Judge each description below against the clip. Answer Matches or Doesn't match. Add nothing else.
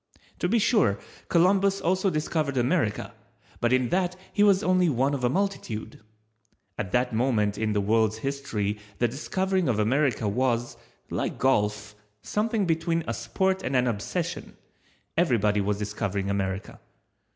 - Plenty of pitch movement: Matches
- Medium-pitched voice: Doesn't match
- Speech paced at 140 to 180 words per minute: Matches